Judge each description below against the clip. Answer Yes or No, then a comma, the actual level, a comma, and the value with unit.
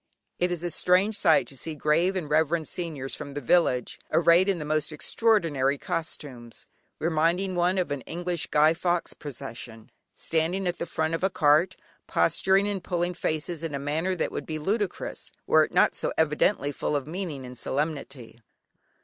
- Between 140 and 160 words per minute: No, average, 175 wpm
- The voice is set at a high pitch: No, medium, 160 Hz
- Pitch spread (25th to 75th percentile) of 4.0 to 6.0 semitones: No, average, 3.4 semitones